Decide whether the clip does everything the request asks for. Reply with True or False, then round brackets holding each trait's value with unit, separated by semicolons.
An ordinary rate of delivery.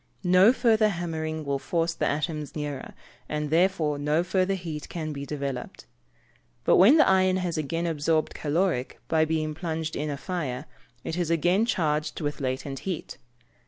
True (160 wpm)